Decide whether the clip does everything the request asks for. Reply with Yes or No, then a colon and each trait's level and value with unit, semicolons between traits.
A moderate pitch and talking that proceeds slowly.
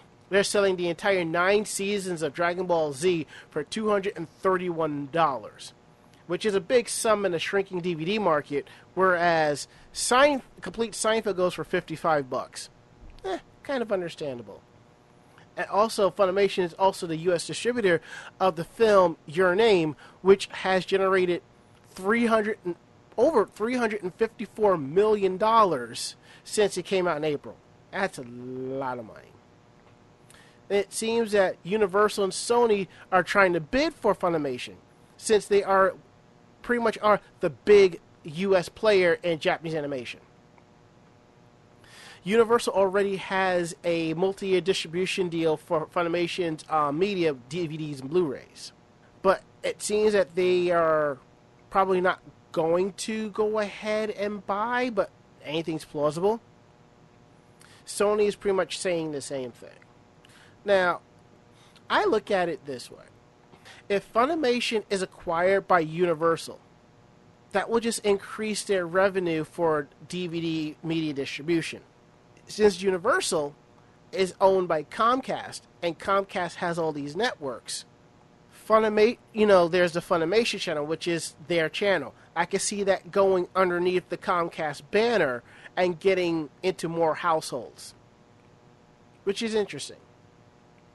Yes: medium, 180 Hz; slow, 125 wpm